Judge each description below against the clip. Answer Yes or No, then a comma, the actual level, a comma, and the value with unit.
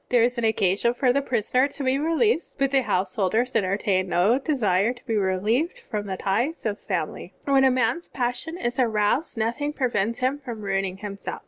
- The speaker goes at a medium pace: Yes, average, 195 wpm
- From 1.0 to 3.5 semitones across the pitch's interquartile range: No, average, 4.7 semitones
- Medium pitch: No, high, 235 Hz